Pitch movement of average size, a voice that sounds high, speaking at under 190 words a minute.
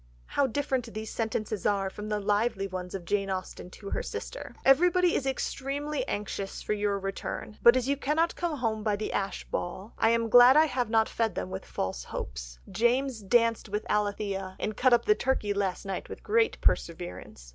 No: average, 4.8 semitones; high, 215 Hz; average, 195 wpm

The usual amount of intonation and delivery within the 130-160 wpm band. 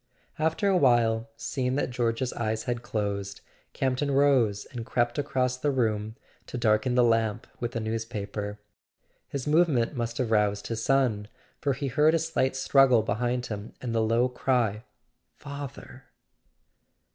Yes: average, 3.2 semitones; average, 150 wpm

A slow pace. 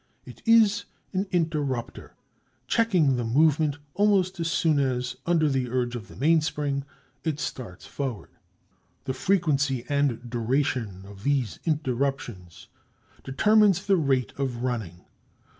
Yes: slow, 125 wpm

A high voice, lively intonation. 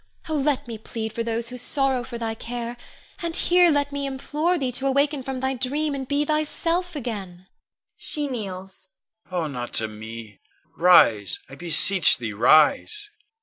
Yes: high, 245 Hz; wide, 7.8 semitones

